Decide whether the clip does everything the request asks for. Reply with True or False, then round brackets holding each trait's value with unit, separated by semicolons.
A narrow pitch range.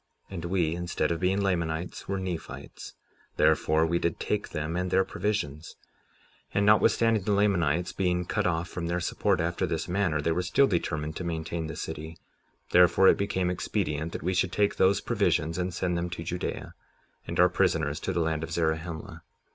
True (2.3 semitones)